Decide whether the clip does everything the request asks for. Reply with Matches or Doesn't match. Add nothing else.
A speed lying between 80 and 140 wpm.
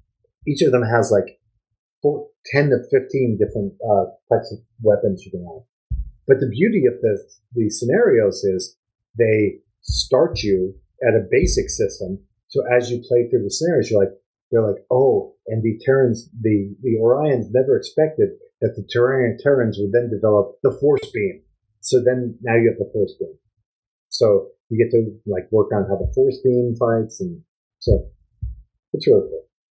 Doesn't match